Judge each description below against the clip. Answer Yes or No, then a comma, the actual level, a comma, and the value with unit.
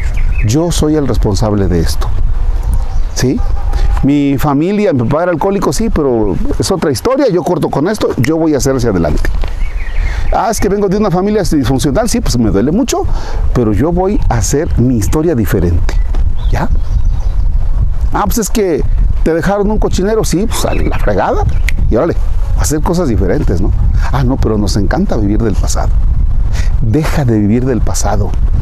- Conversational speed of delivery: Yes, average, 170 wpm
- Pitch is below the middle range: Yes, low, 105 Hz